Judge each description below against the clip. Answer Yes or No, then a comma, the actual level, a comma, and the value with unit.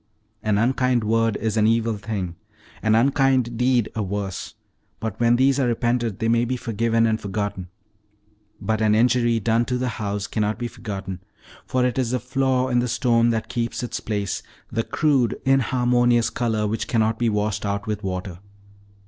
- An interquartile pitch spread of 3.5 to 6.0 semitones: No, narrow, 2.5 semitones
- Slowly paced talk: No, average, 175 wpm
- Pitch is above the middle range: No, low, 115 Hz